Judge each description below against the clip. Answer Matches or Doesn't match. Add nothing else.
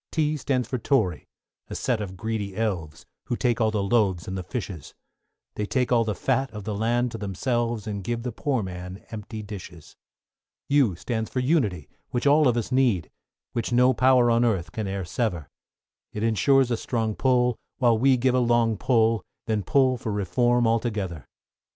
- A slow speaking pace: Doesn't match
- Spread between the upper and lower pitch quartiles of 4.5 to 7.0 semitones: Doesn't match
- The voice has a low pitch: Matches